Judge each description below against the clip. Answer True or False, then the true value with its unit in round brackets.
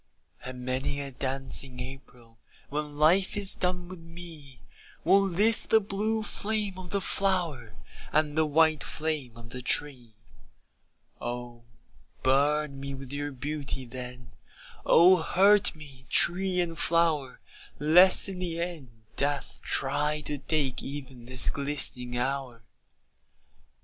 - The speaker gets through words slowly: True (130 wpm)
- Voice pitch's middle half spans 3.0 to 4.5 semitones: False (5.0 semitones)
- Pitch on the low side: False (145 Hz)